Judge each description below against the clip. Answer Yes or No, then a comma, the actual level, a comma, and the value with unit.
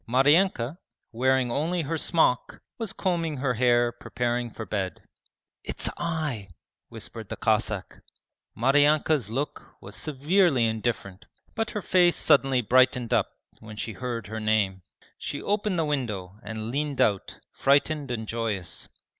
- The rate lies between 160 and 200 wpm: No, average, 140 wpm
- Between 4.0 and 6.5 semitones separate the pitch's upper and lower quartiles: Yes, average, 5.3 semitones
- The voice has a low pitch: Yes, low, 125 Hz